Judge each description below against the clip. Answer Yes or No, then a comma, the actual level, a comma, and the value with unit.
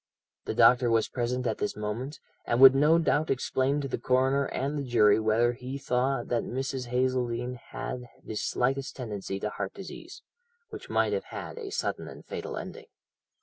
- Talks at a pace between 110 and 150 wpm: No, average, 180 wpm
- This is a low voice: Yes, low, 125 Hz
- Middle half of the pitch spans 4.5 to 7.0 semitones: No, narrow, 2.5 semitones